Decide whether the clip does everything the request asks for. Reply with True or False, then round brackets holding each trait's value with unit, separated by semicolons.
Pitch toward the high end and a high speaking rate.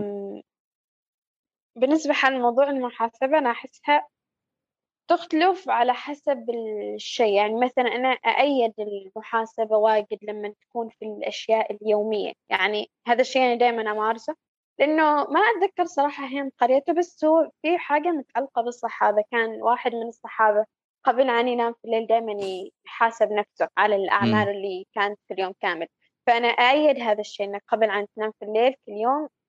True (235 Hz; 140 wpm)